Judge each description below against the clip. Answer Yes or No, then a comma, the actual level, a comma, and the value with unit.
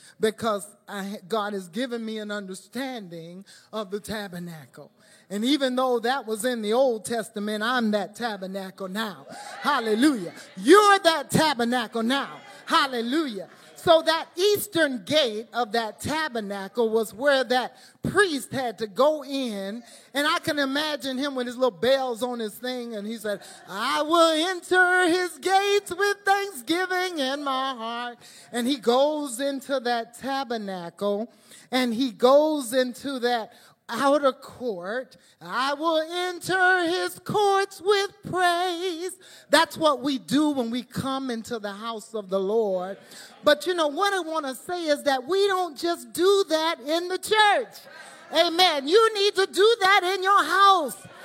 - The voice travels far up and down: Yes, wide, 6.6 semitones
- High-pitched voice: Yes, very high, 265 Hz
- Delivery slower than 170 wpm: Yes, average, 155 wpm